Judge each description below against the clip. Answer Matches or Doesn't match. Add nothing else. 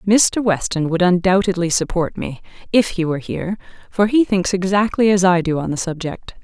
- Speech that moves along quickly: Doesn't match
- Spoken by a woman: Matches